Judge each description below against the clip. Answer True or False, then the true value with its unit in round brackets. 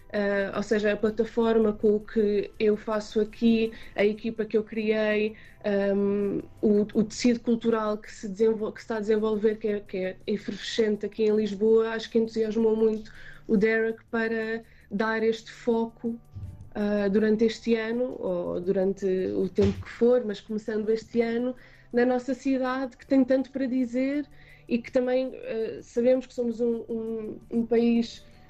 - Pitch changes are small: True (1.8 semitones)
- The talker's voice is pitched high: True (225 Hz)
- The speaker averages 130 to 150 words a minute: False (170 wpm)